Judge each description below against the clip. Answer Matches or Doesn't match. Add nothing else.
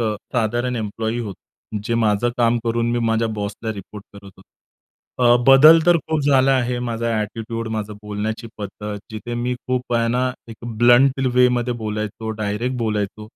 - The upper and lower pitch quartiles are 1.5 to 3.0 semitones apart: Matches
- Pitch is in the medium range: Doesn't match